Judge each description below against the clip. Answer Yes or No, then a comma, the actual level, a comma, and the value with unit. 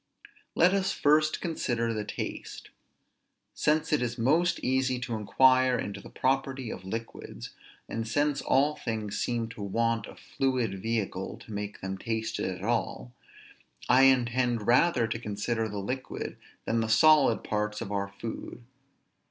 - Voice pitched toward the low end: Yes, low, 115 Hz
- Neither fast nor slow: Yes, average, 150 wpm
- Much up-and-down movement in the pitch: No, average, 3.7 semitones